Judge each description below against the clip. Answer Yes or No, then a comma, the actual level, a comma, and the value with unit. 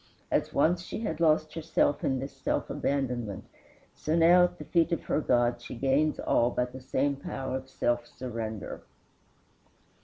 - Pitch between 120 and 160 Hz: Yes, low, 135 Hz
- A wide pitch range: No, average, 4.4 semitones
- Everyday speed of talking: Yes, average, 165 wpm